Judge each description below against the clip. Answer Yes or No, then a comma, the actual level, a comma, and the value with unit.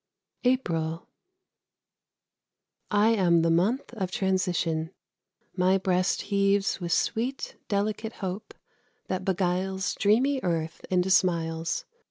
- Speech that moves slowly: Yes, slow, 100 wpm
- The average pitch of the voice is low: No, high, 190 Hz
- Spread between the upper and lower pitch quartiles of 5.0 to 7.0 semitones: No, average, 2.9 semitones